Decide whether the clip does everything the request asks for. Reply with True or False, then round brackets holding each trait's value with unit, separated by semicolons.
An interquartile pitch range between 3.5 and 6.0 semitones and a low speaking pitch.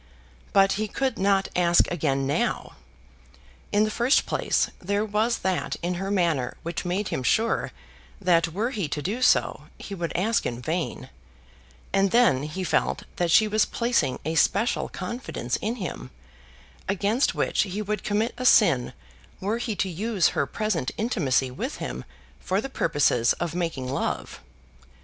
False (4.8 semitones; 190 Hz)